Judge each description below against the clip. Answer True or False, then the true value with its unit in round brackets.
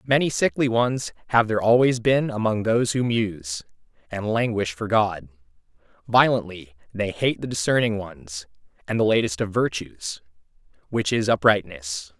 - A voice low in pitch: True (105 Hz)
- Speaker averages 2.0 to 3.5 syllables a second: False (4.7 syllables/s)